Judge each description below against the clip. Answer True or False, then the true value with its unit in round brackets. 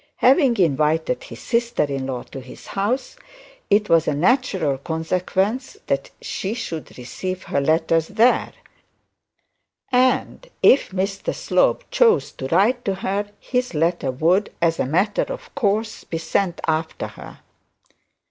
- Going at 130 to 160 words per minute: True (140 wpm)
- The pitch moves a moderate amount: False (6.5 semitones)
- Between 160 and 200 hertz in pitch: True (185 Hz)